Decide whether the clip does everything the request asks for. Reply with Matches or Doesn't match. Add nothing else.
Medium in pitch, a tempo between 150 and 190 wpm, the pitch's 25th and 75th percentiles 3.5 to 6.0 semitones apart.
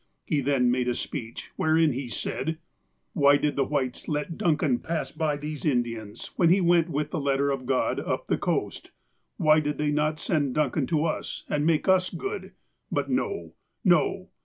Doesn't match